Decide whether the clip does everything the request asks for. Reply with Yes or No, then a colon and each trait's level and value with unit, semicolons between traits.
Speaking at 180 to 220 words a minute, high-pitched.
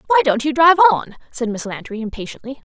Yes: average, 200 wpm; very high, 270 Hz